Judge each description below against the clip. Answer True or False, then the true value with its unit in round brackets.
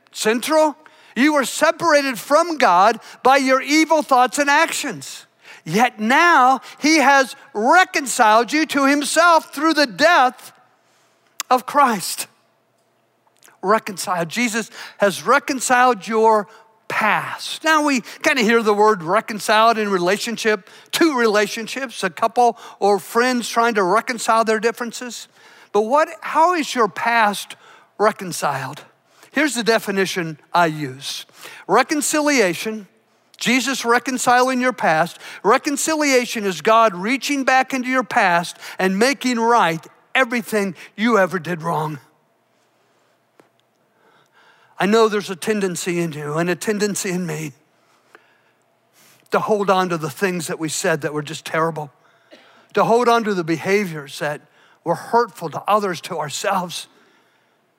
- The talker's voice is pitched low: False (225 Hz)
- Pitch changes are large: True (5.8 semitones)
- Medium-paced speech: False (130 wpm)